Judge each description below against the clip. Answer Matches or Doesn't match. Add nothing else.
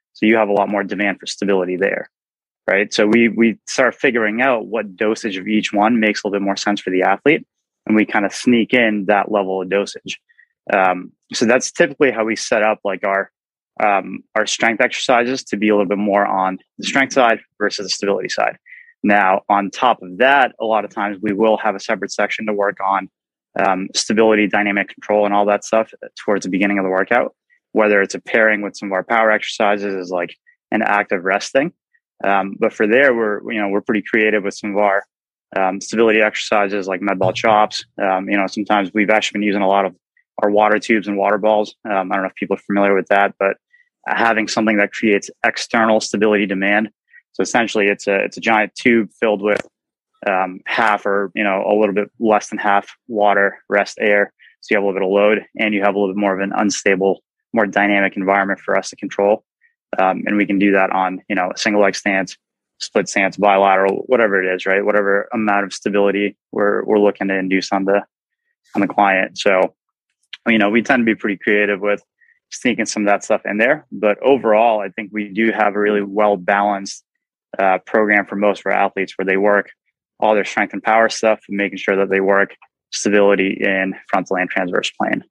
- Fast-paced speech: Matches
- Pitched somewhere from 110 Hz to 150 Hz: Doesn't match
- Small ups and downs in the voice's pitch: Matches